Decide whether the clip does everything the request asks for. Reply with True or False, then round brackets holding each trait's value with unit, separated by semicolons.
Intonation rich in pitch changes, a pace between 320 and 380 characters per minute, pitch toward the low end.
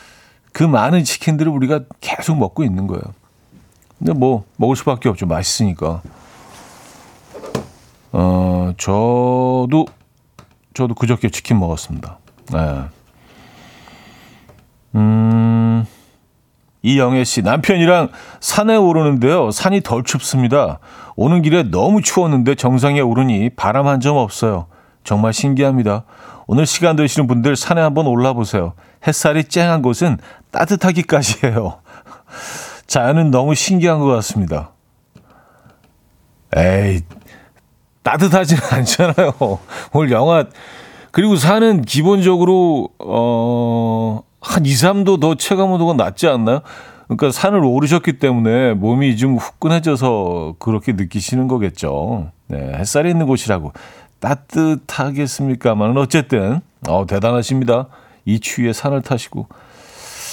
False (6.0 semitones; 255 characters per minute; 130 Hz)